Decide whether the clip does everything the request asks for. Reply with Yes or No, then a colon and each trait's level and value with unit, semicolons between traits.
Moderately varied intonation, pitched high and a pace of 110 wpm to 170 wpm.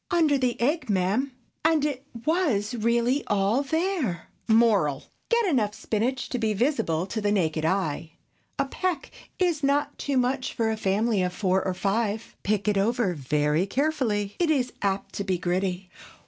No: wide, 6.3 semitones; high, 220 Hz; average, 160 wpm